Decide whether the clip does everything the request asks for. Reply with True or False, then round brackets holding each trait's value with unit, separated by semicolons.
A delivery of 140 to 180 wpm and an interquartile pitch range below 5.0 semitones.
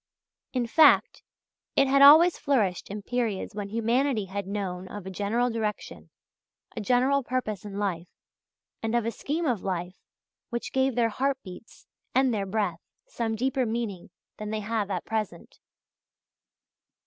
True (150 wpm; 4.1 semitones)